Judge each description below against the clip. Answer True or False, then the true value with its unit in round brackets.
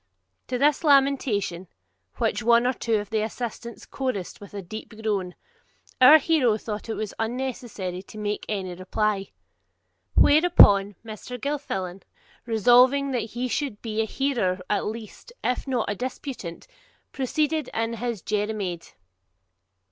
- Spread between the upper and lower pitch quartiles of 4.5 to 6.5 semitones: False (4.0 semitones)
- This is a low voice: False (225 Hz)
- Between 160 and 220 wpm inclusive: False (135 wpm)